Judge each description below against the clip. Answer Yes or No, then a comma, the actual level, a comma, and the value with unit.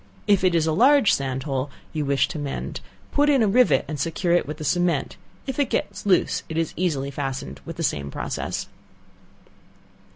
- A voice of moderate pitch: Yes, medium, 160 Hz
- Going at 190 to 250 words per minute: Yes, average, 195 wpm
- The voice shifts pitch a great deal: Yes, wide, 6.2 semitones